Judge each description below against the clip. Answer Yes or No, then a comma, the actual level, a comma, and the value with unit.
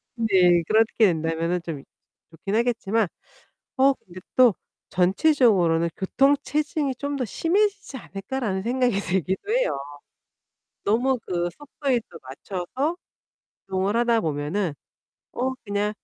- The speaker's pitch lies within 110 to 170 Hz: No, high, 210 Hz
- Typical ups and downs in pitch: No, wide, 6.7 semitones